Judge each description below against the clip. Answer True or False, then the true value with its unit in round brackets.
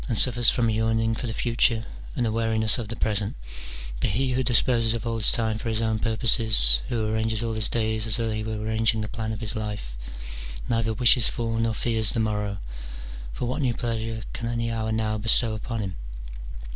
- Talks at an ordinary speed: False (210 wpm)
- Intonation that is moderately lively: False (1.1 semitones)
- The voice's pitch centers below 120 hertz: True (110 Hz)